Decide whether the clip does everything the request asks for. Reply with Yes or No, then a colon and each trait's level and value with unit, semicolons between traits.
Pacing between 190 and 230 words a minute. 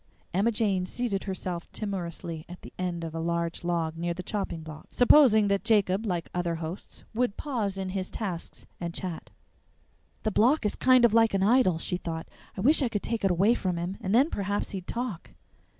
Yes: average, 200 wpm